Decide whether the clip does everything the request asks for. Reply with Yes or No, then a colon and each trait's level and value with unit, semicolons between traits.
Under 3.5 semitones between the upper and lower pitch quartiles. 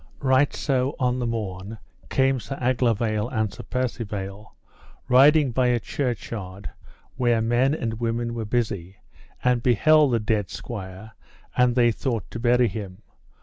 Yes: average, 2.9 semitones